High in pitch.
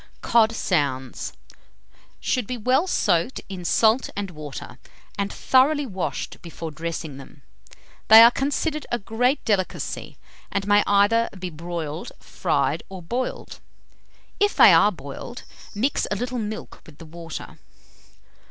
Yes: high, 200 Hz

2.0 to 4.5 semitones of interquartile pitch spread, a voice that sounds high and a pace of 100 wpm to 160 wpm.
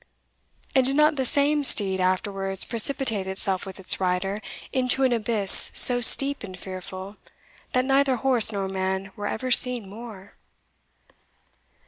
No: average, 5.1 semitones; high, 210 Hz; average, 140 wpm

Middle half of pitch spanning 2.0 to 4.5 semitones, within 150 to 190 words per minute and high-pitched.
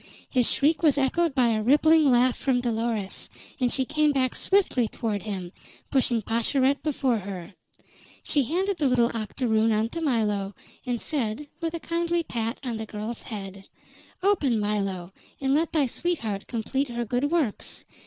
No: average, 5.1 semitones; average, 165 wpm; high, 245 Hz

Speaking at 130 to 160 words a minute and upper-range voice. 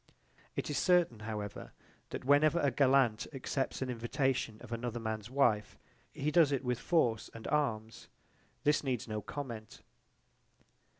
No: average, 140 wpm; low, 125 Hz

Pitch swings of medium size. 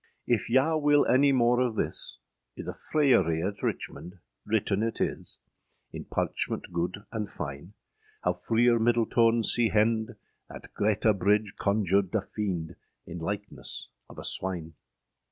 Yes: average, 3.9 semitones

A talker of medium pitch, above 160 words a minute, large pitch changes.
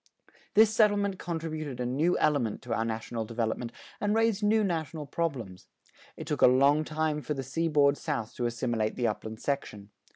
Yes: medium, 145 Hz; average, 170 wpm; wide, 5.9 semitones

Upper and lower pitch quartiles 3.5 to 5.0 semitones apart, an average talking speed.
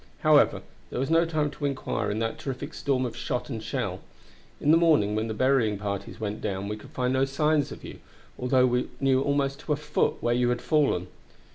No: average, 4.3 semitones; fast, 220 wpm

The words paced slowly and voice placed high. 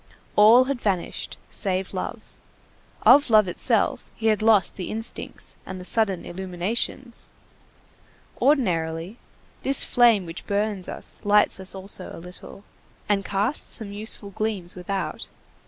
Yes: slow, 130 wpm; high, 200 Hz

